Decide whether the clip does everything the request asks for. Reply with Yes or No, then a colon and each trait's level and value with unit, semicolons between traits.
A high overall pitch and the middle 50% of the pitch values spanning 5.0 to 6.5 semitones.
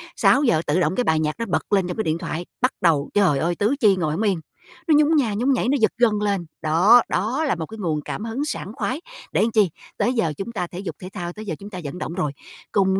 Yes: high, 195 Hz; average, 5.3 semitones